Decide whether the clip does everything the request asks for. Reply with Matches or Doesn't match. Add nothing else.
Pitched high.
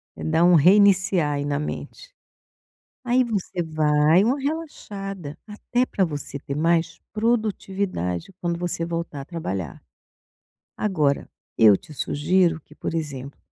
Doesn't match